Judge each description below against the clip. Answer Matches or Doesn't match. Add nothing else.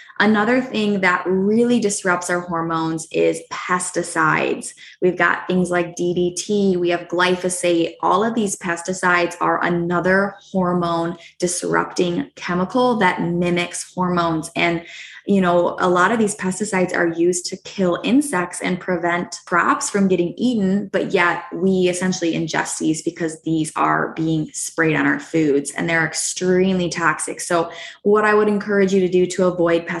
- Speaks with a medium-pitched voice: Matches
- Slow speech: Doesn't match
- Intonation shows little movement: Matches